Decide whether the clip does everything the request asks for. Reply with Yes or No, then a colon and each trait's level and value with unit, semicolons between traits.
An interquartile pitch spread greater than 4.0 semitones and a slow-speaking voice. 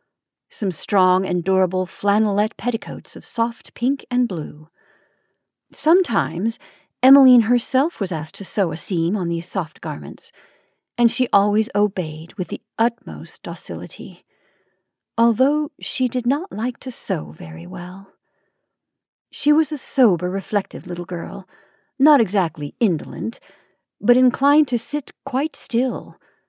Yes: wide, 5.5 semitones; slow, 130 wpm